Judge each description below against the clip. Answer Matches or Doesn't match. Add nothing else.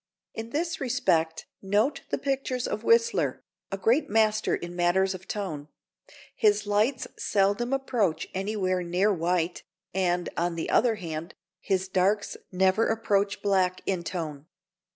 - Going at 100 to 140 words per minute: Matches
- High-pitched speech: Matches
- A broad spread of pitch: Doesn't match